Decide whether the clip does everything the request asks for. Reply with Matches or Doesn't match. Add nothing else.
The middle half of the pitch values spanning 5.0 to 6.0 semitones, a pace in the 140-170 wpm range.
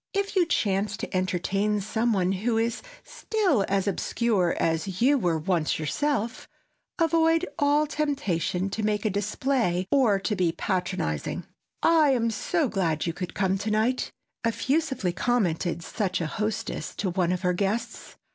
Matches